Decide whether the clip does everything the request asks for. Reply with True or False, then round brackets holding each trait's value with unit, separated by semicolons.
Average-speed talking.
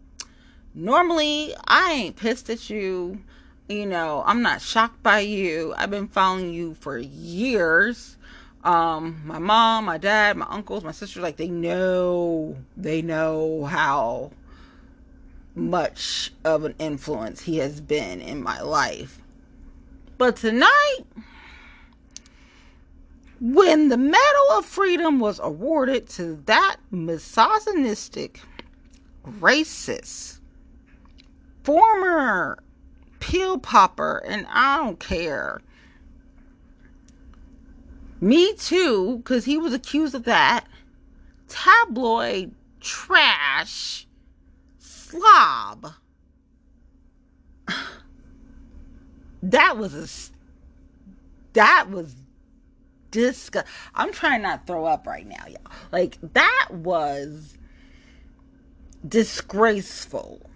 False (95 wpm)